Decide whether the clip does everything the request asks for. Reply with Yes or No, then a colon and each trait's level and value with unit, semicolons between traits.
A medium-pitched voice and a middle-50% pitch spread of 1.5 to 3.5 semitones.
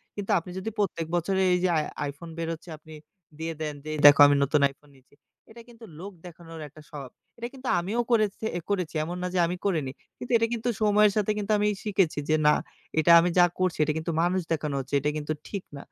No: medium, 170 Hz; average, 4.8 semitones